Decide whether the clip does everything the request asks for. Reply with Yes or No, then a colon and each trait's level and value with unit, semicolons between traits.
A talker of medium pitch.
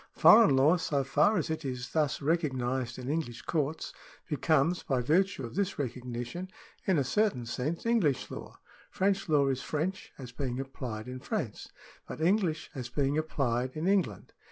Yes: medium, 145 Hz